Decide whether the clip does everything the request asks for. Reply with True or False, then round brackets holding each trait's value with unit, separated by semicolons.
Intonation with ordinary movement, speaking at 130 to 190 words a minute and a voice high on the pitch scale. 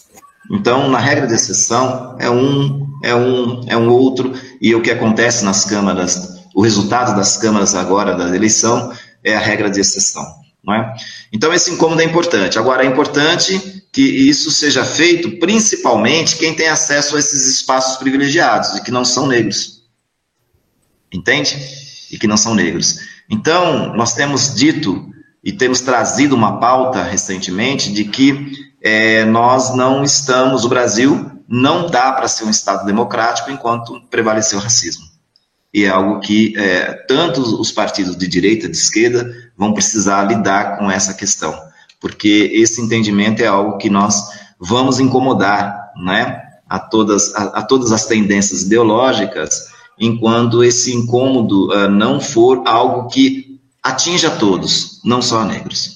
False (4.9 semitones; 155 wpm; 120 Hz)